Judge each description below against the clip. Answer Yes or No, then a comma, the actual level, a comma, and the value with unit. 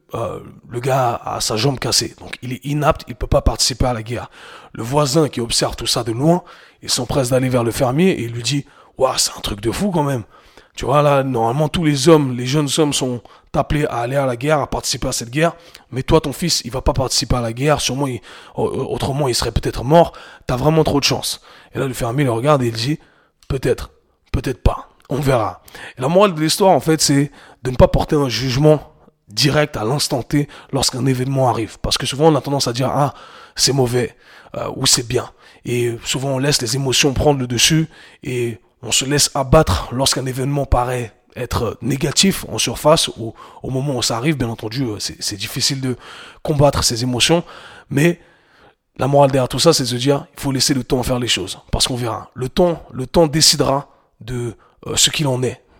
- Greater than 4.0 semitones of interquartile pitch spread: No, average, 3.4 semitones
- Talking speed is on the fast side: Yes, fast, 225 wpm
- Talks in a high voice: No, low, 135 Hz